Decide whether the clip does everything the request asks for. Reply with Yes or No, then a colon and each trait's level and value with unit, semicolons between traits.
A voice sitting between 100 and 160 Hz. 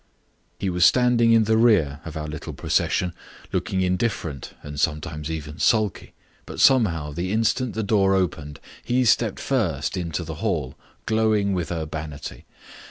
No: very low, 90 Hz